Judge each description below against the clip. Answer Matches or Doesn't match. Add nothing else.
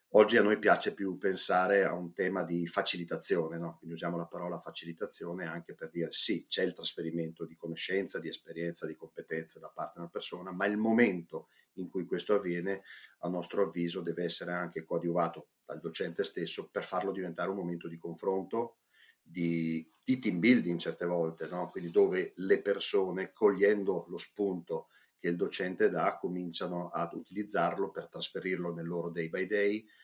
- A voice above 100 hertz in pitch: Doesn't match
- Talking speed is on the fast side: Matches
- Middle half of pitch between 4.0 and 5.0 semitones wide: Doesn't match